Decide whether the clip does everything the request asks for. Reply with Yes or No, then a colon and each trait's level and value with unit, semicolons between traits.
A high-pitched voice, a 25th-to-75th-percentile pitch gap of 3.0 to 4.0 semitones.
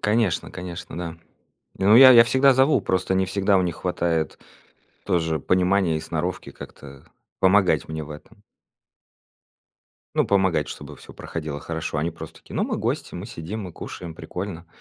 No: very low, 90 Hz; average, 3.6 semitones